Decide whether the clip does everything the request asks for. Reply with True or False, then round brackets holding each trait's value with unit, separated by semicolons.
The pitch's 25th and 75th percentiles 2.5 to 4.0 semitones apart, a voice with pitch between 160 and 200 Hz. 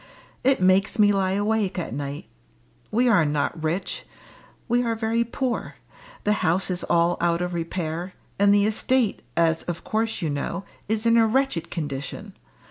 False (4.8 semitones; 190 Hz)